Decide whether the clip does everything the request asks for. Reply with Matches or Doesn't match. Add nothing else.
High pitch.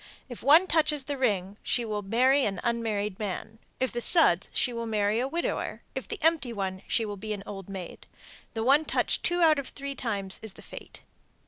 Matches